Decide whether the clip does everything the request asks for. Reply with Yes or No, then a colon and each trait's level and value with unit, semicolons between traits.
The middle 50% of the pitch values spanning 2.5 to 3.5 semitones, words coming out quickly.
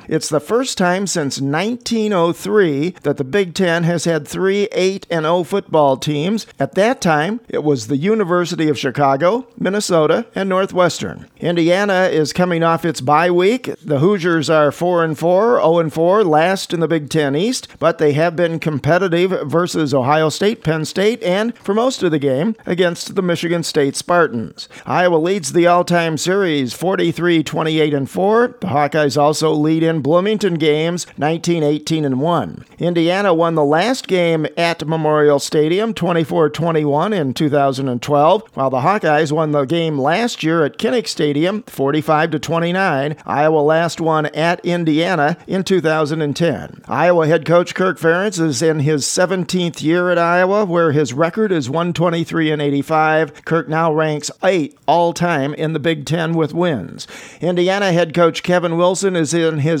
No: average, 2.8 semitones; average, 160 wpm